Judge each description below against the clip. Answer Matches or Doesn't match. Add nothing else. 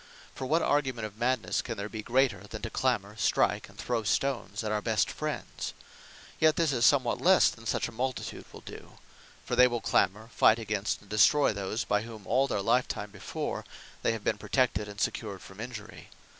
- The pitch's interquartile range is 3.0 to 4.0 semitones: Matches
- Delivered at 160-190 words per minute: Doesn't match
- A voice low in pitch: Matches